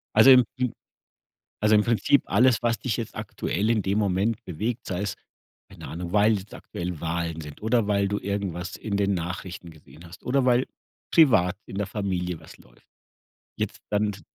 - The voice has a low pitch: Yes, low, 100 Hz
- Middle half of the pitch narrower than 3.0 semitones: No, average, 4.0 semitones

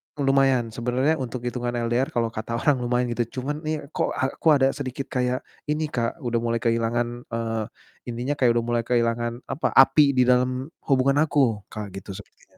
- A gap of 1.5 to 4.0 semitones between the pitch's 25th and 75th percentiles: Yes, narrow, 2.5 semitones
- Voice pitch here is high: No, low, 125 Hz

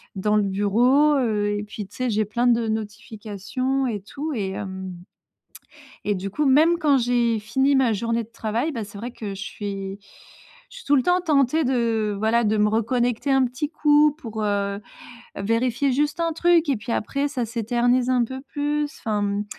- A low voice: No, high, 235 Hz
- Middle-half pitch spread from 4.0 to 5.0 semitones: Yes, average, 4.6 semitones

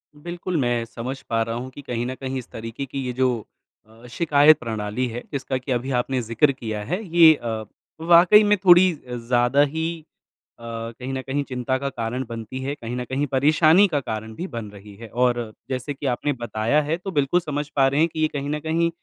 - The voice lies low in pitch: Yes, low, 130 Hz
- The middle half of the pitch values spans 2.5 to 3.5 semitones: No, average, 4.3 semitones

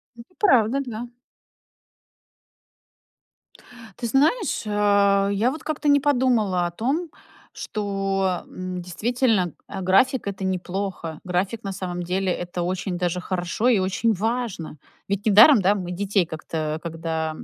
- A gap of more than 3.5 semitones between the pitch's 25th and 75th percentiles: Yes, average, 4.5 semitones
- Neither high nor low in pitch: No, high, 195 Hz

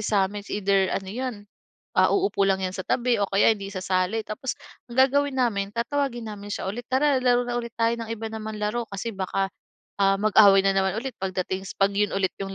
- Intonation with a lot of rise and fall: No, average, 3.5 semitones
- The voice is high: Yes, high, 210 Hz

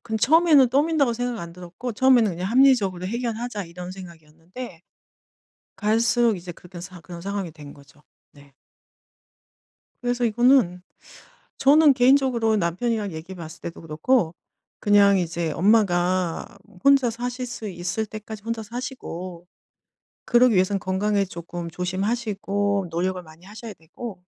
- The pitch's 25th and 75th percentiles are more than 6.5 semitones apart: No, average, 5.3 semitones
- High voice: Yes, high, 200 Hz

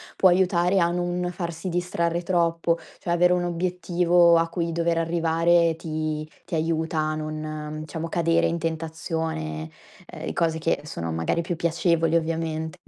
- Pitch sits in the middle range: Yes, medium, 165 Hz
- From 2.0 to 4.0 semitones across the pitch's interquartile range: No, narrow, 1.3 semitones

